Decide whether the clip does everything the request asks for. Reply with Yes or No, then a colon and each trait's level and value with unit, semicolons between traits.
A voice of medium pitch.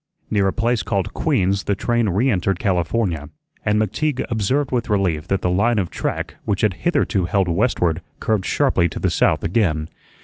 No: low, 100 Hz